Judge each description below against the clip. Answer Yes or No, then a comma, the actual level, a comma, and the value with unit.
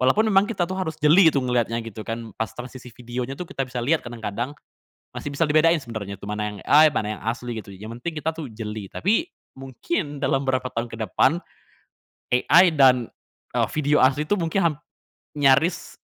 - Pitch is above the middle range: No, low, 135 Hz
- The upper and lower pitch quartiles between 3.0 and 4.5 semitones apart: No, average, 5.1 semitones